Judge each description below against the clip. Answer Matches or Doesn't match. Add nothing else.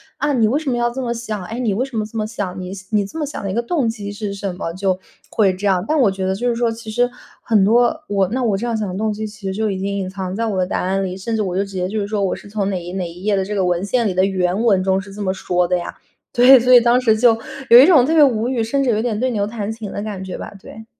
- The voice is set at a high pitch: Matches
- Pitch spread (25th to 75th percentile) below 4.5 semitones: Matches